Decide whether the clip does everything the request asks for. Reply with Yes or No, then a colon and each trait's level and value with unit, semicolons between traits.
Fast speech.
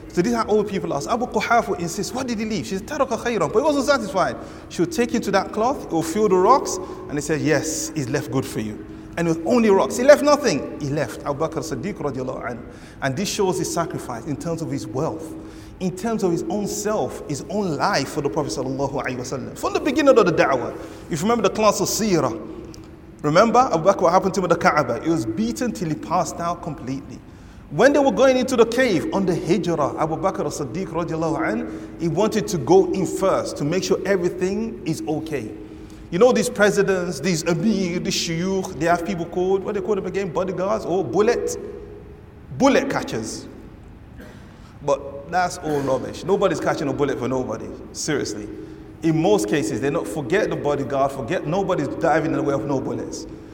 Yes: fast, 210 wpm